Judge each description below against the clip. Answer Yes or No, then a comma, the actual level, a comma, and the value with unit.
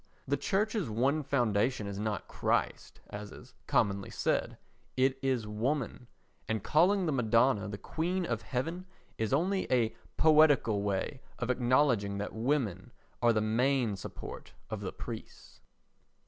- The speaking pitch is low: Yes, low, 125 Hz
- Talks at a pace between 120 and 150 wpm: Yes, average, 140 wpm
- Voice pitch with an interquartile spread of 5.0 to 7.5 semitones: Yes, wide, 5.4 semitones